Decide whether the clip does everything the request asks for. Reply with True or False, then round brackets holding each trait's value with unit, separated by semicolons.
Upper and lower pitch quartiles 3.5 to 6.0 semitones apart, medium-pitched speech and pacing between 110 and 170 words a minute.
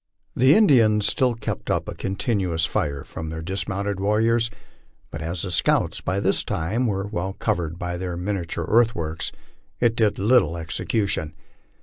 False (4.8 semitones; 95 Hz; 155 wpm)